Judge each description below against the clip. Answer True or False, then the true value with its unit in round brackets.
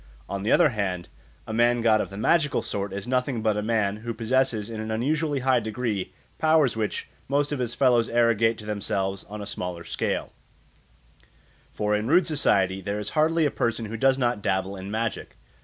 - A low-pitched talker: True (115 Hz)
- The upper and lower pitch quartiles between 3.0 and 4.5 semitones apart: True (3.7 semitones)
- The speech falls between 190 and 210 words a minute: True (195 wpm)